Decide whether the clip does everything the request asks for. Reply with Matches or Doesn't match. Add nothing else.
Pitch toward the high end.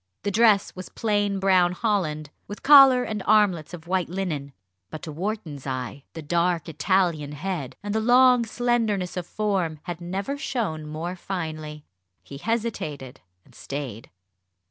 Doesn't match